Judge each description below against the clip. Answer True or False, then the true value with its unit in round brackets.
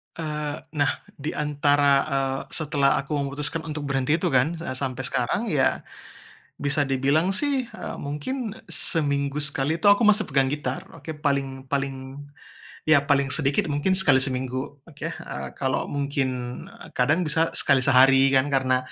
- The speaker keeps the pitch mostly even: True (2.2 semitones)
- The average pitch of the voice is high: False (140 Hz)